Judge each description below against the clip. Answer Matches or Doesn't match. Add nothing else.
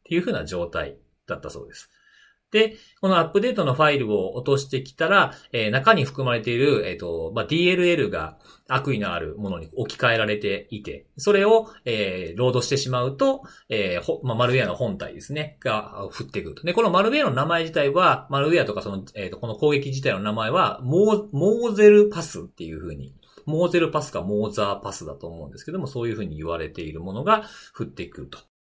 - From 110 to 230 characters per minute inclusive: Doesn't match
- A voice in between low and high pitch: Matches